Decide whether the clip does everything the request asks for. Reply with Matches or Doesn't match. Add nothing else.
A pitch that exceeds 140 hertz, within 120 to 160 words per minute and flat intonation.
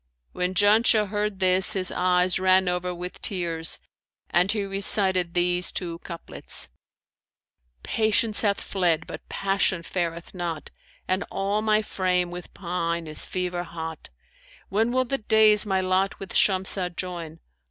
Matches